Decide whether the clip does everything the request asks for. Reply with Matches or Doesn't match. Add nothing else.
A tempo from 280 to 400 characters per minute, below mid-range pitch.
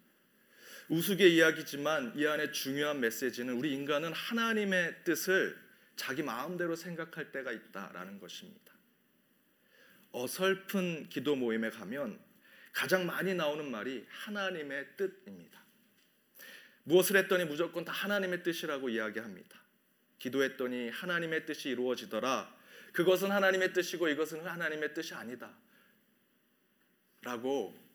Doesn't match